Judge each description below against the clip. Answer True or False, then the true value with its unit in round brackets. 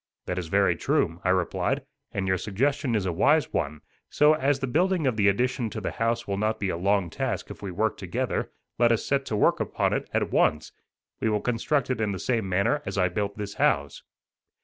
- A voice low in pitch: True (105 Hz)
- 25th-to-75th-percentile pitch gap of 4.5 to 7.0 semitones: True (5.2 semitones)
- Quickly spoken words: True (225 wpm)